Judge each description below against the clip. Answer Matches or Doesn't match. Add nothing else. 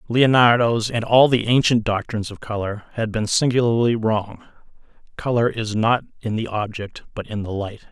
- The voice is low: Matches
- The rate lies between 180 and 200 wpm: Doesn't match